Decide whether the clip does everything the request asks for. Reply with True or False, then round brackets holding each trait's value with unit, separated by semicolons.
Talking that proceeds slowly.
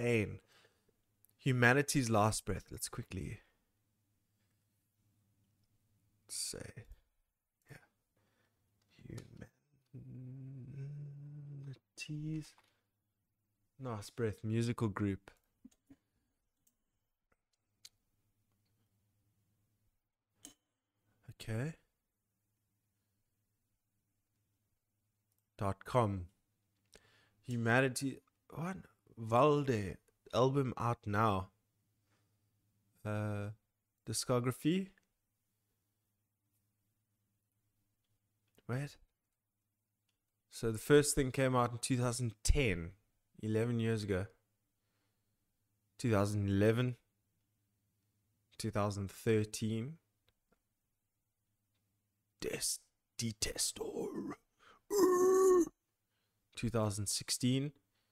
True (45 wpm)